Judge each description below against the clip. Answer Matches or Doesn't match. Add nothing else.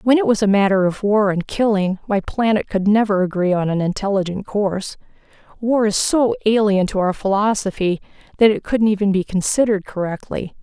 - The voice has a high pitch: Matches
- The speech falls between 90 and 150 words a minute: Doesn't match